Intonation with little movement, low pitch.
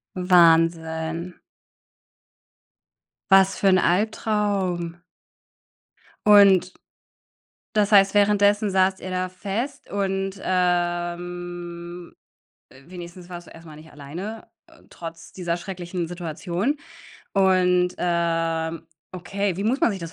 No: narrow, 2.3 semitones; medium, 180 Hz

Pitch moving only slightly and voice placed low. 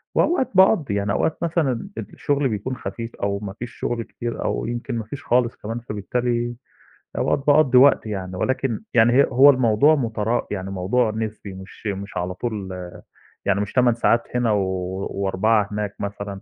No: average, 3.8 semitones; low, 115 Hz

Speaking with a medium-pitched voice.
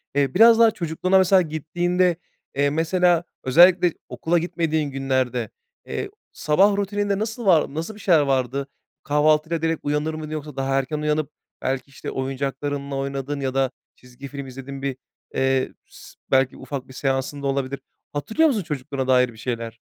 Yes: medium, 145 Hz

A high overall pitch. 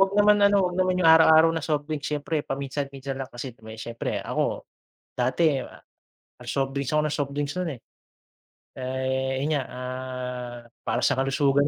No: medium, 140 Hz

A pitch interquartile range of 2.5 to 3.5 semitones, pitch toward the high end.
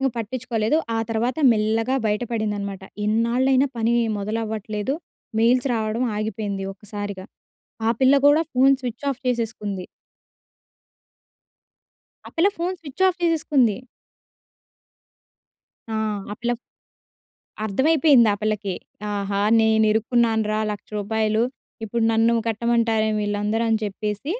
Yes: average, 2.9 semitones; high, 225 Hz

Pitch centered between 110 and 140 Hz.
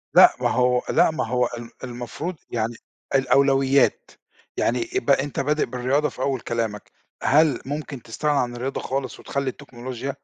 Yes: low, 135 Hz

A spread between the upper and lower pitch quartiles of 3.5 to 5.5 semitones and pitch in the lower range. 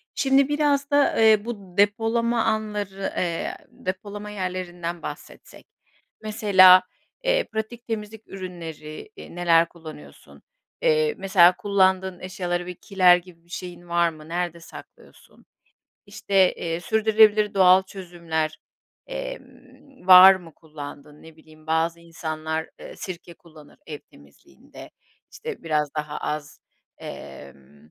No: average, 4.1 semitones; medium, 180 Hz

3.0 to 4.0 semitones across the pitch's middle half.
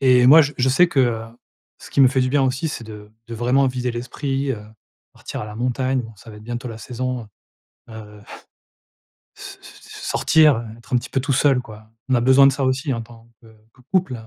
No: narrow, 2.6 semitones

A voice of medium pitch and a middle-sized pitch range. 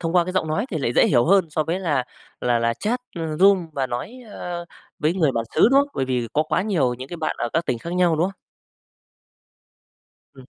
No: medium, 160 Hz; wide, 5.7 semitones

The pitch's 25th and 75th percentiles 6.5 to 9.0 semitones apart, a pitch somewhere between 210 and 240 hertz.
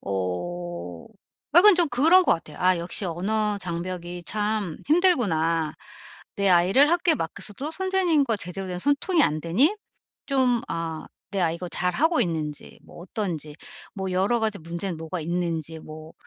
No: wide, 7.1 semitones; medium, 185 Hz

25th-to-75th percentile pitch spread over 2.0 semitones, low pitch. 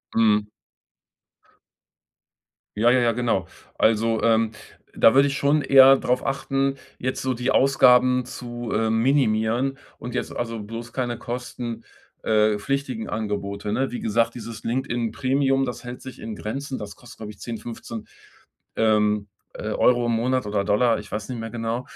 Yes: average, 2.7 semitones; low, 120 Hz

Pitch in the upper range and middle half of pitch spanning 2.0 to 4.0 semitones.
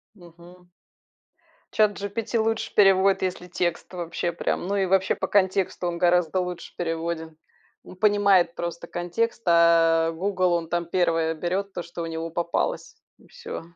No: medium, 175 Hz; narrow, 2.4 semitones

